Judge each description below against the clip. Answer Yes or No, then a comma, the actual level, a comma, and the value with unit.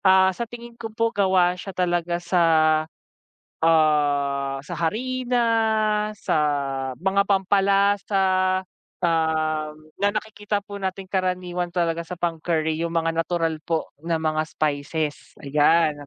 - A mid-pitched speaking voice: Yes, medium, 175 Hz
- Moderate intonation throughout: Yes, average, 3.5 semitones